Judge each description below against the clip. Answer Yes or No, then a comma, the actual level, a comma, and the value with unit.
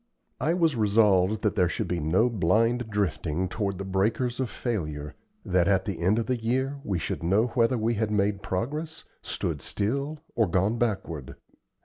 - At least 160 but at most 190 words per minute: Yes, average, 175 wpm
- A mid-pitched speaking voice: No, low, 105 Hz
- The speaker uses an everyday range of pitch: Yes, average, 4.5 semitones